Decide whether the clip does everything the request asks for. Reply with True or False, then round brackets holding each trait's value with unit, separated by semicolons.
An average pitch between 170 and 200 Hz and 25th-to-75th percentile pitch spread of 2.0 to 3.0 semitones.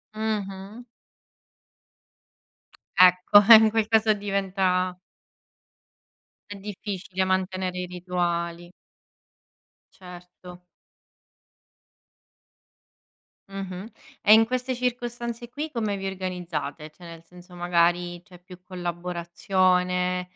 True (185 Hz; 2.6 semitones)